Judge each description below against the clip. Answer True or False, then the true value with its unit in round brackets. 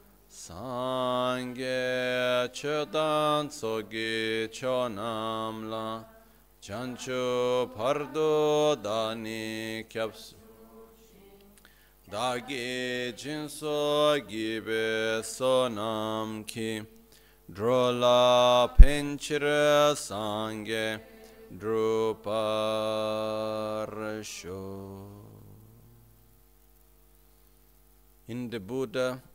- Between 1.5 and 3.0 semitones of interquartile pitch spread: True (2.7 semitones)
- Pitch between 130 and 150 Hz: False (115 Hz)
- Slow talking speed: True (45 wpm)